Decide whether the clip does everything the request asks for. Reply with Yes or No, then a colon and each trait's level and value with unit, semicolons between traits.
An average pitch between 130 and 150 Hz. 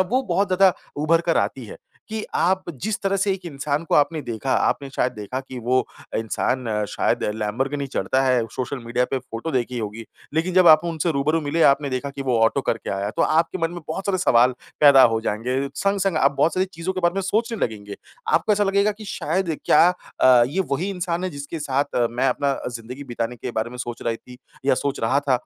Yes: medium, 140 Hz